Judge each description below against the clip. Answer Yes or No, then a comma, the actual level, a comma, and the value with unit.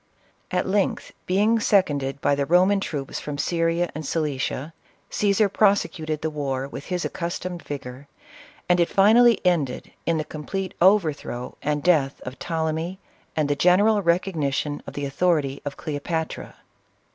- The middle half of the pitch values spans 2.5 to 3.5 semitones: No, average, 4.2 semitones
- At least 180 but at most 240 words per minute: No, average, 145 wpm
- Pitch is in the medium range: Yes, medium, 160 Hz